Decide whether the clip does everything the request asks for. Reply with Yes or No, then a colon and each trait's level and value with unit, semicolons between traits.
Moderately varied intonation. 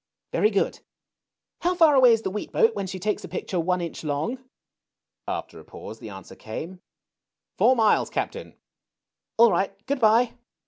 No: wide, 6.5 semitones